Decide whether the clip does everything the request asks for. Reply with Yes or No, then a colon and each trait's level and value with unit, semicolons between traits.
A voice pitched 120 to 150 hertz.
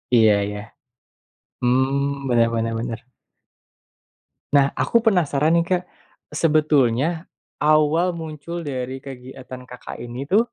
Yes: medium, 140 Hz